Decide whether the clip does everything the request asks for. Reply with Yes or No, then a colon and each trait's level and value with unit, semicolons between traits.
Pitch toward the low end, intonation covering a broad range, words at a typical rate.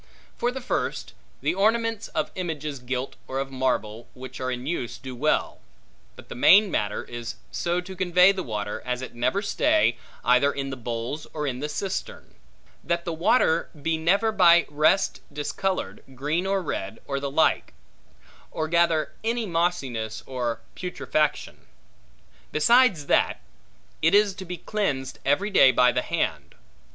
No: medium, 155 Hz; wide, 6.4 semitones; average, 160 wpm